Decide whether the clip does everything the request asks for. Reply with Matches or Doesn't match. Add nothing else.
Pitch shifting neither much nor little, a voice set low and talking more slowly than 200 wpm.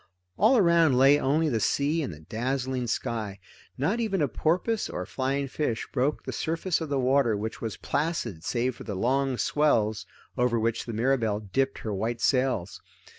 Matches